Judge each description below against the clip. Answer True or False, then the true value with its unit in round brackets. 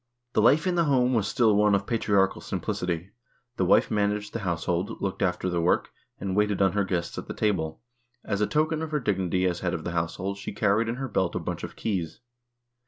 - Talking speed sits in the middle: False (230 wpm)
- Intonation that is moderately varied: True (3.6 semitones)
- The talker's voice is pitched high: False (100 Hz)